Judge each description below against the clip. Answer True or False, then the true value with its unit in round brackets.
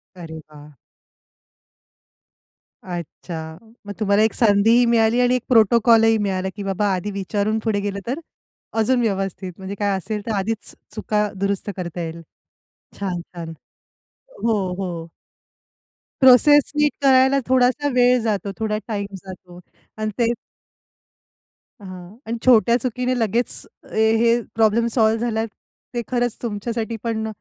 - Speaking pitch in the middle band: False (220 Hz)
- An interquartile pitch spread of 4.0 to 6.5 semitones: False (3.4 semitones)